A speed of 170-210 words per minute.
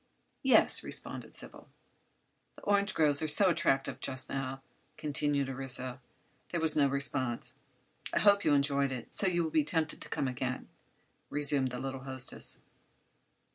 No: average, 150 wpm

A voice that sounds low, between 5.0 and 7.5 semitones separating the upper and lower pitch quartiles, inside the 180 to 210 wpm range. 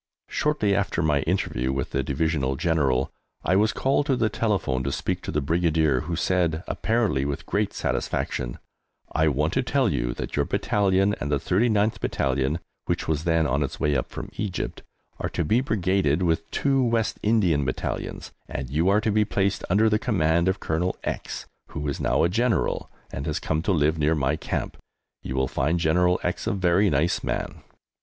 Yes: very low, 85 Hz; wide, 5.6 semitones; average, 190 wpm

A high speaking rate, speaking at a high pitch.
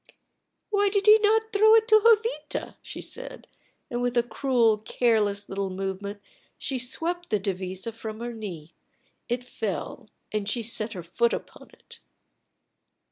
No: average, 150 wpm; high, 235 Hz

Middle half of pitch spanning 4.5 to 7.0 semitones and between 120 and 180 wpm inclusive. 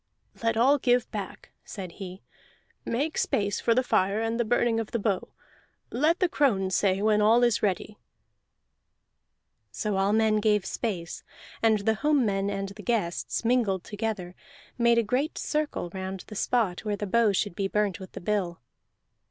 No: average, 3.2 semitones; average, 170 wpm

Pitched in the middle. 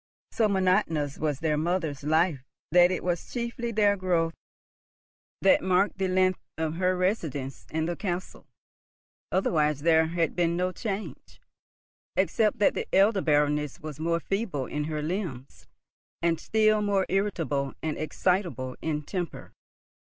Yes: medium, 175 Hz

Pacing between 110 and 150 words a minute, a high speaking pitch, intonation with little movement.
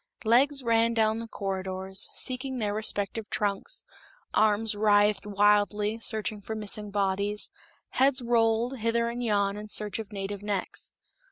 Yes: average, 140 wpm; high, 210 Hz; narrow, 2.0 semitones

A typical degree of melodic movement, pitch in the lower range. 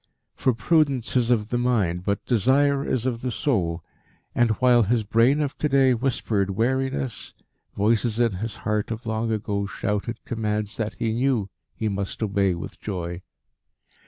Yes: average, 3.5 semitones; low, 115 Hz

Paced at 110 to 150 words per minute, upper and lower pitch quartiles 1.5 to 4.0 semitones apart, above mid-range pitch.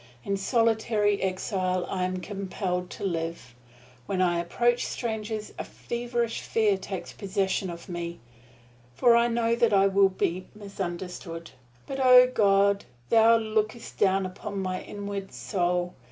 Yes: average, 140 wpm; average, 3.3 semitones; high, 195 Hz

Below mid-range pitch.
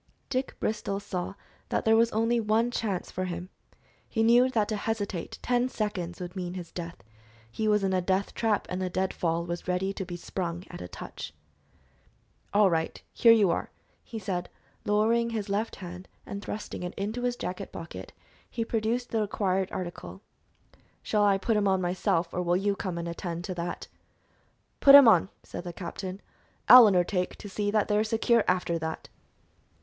No: high, 195 Hz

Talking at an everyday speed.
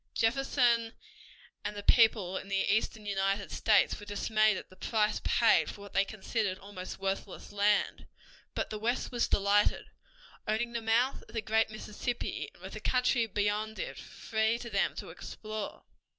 Yes: average, 165 wpm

